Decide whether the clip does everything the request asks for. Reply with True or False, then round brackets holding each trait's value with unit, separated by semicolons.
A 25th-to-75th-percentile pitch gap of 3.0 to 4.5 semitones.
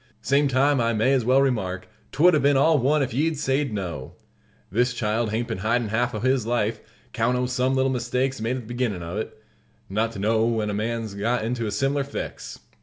True (3.5 semitones)